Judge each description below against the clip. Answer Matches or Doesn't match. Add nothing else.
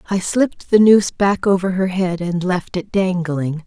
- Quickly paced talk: Doesn't match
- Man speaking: Doesn't match